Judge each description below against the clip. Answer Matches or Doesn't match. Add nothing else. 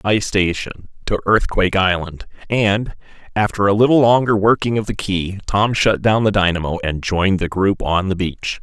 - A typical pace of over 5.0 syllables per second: Doesn't match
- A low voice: Matches